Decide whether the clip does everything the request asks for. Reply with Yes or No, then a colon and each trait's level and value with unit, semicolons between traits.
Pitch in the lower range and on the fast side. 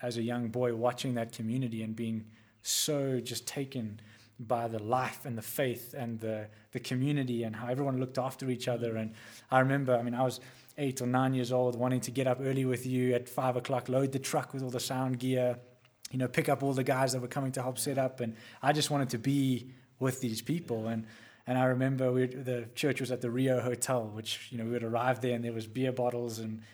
Yes: low, 125 Hz; fast, 240 wpm